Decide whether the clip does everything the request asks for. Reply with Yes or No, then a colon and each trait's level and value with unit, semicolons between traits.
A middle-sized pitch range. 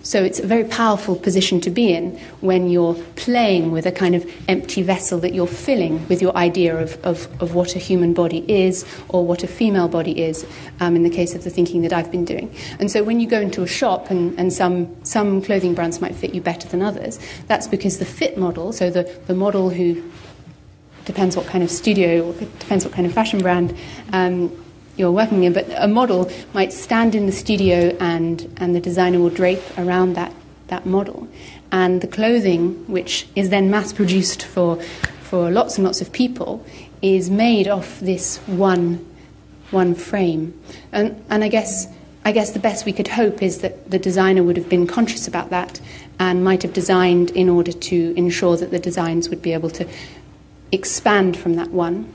No: narrow, 1.9 semitones